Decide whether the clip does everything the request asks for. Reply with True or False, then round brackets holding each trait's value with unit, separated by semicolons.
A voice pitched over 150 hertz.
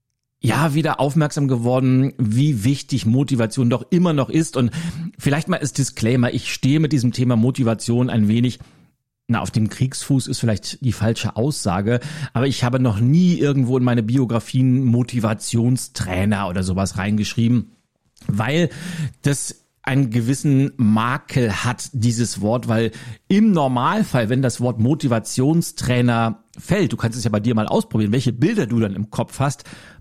False (125 Hz)